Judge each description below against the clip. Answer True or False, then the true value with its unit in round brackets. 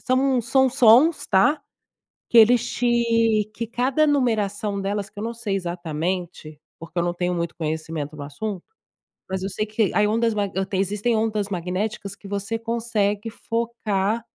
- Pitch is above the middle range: True (210 Hz)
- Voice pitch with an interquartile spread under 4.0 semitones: True (3.6 semitones)